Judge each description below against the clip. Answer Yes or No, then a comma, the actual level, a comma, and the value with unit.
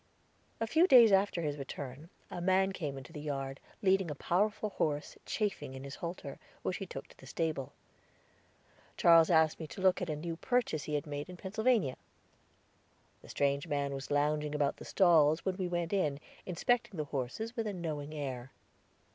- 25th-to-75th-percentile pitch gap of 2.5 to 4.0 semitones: No, average, 4.7 semitones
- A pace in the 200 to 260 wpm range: No, average, 185 wpm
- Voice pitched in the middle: Yes, medium, 160 Hz